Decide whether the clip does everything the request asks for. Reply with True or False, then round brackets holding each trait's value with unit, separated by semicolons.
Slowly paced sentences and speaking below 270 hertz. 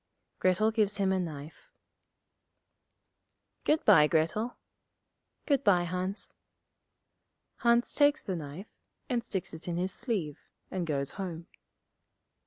True (115 wpm; 185 Hz)